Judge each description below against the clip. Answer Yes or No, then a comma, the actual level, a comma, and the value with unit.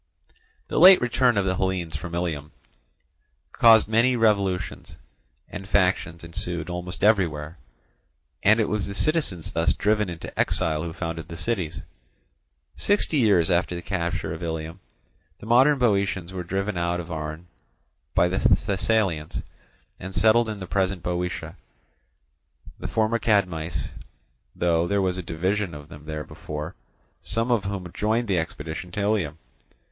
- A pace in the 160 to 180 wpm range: No, average, 145 wpm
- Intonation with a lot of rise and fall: No, average, 4.1 semitones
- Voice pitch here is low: Yes, very low, 90 Hz